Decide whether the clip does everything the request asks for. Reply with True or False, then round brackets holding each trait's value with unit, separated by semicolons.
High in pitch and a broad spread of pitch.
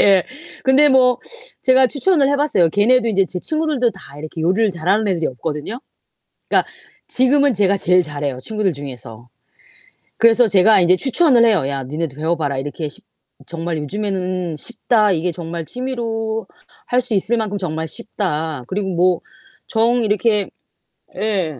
True (195 Hz; 6.3 semitones)